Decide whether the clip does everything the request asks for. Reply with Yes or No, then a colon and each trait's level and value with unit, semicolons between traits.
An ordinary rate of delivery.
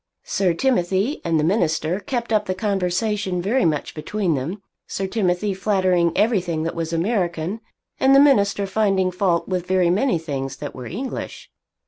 Yes: average, 160 wpm